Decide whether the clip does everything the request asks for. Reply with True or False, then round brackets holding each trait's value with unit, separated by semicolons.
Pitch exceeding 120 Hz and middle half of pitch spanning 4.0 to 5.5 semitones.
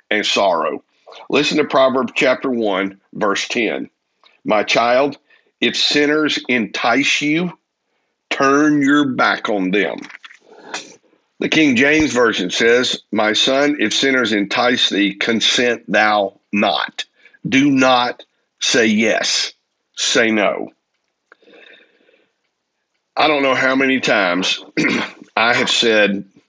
True (135 Hz; 5.1 semitones)